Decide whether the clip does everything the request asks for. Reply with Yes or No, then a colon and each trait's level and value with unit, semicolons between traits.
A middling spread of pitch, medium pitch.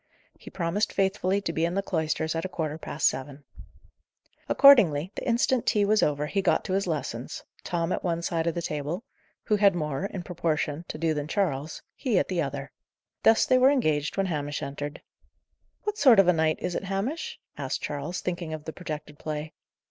Yes: average, 4.4 semitones; medium, 170 Hz